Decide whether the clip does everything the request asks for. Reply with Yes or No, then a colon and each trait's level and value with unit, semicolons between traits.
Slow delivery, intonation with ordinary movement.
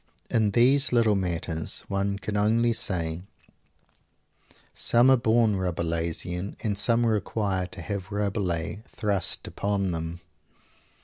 Yes: slow, 115 wpm; average, 3.9 semitones